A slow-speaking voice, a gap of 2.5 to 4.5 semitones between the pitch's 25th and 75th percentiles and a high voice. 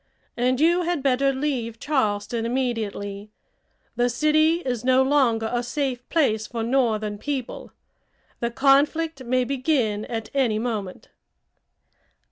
Yes: slow, 120 wpm; average, 3.6 semitones; very high, 250 Hz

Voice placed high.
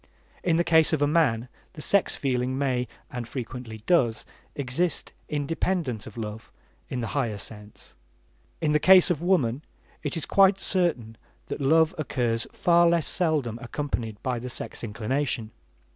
No: low, 135 Hz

